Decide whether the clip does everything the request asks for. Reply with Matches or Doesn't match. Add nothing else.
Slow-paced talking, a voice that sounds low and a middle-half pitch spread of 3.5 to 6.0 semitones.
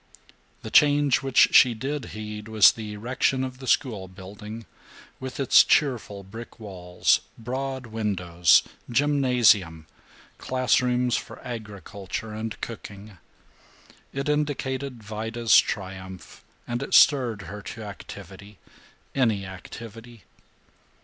Matches